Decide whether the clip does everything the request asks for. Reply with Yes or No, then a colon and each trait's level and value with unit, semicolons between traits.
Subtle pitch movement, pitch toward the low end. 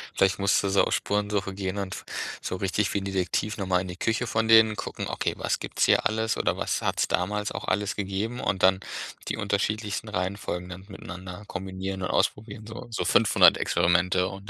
Yes: narrow, 2.1 semitones; low, 100 Hz